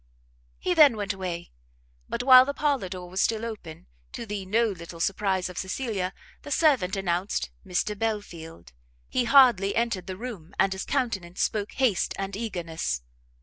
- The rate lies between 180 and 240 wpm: No, average, 160 wpm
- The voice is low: No, high, 195 Hz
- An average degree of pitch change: Yes, average, 4.5 semitones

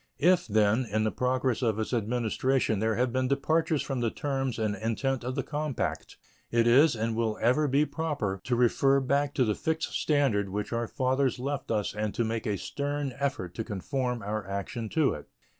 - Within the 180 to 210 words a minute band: Yes, average, 195 wpm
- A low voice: Yes, low, 125 Hz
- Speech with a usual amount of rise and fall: Yes, average, 4.0 semitones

